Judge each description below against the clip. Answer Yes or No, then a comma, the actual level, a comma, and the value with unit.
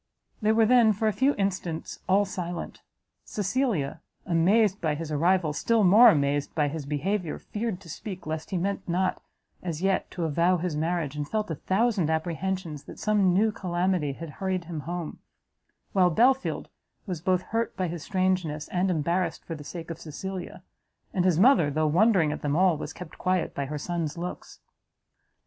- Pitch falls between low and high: Yes, medium, 180 Hz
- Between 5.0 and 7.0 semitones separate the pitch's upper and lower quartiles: No, average, 3.6 semitones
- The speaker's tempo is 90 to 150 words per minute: No, average, 180 wpm